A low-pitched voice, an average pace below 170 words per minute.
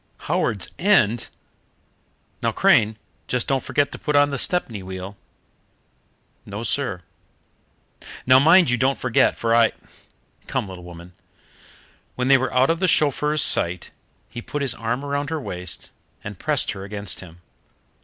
Yes: low, 125 Hz; average, 150 wpm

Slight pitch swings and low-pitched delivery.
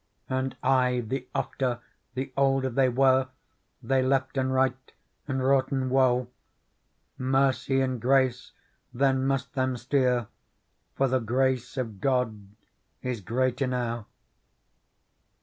Yes: narrow, 1.1 semitones; low, 130 Hz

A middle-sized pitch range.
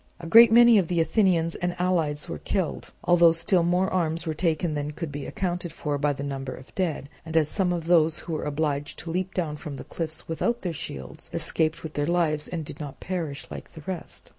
Yes: average, 3.0 semitones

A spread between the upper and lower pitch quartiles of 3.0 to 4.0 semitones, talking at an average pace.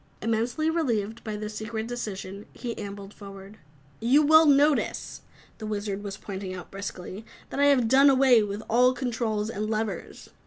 Yes: average, 3.6 semitones; average, 160 wpm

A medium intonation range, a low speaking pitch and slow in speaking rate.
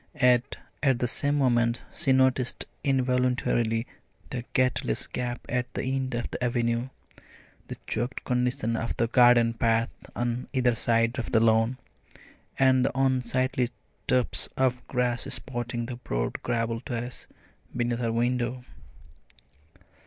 No: narrow, 1.4 semitones; low, 125 Hz; slow, 130 wpm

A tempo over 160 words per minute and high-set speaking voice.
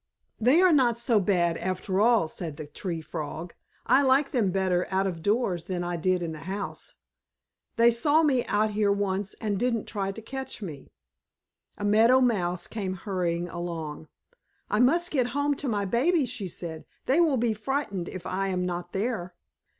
Yes: average, 180 wpm; high, 200 Hz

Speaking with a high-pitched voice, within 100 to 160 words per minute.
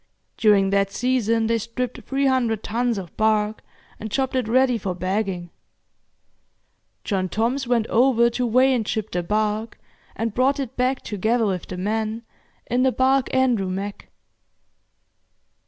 Yes: high, 225 Hz; average, 150 wpm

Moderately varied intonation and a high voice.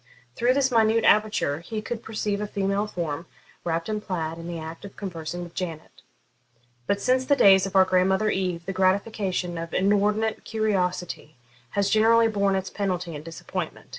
Yes: average, 3.5 semitones; high, 195 Hz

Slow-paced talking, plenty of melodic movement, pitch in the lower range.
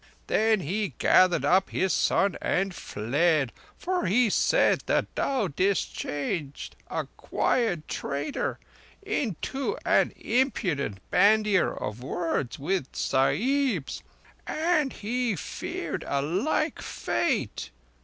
No: slow, 110 wpm; wide, 8.9 semitones; high, 195 Hz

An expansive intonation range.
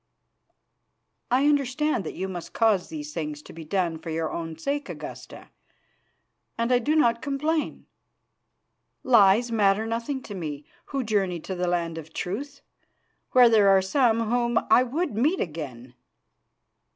Yes: wide, 7.1 semitones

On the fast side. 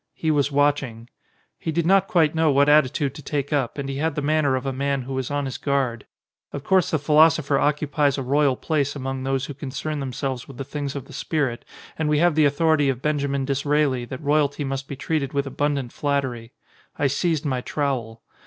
Yes: fast, 210 wpm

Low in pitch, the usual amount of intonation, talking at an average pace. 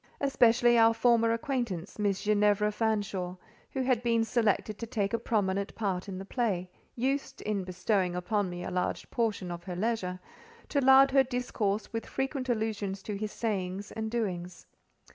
No: high, 215 Hz; average, 3.6 semitones; average, 160 wpm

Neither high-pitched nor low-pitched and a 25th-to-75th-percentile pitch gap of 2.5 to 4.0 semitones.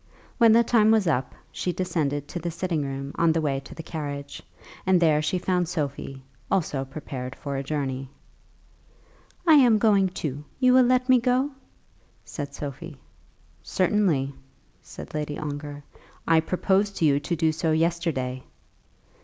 No: medium, 160 Hz; average, 4.9 semitones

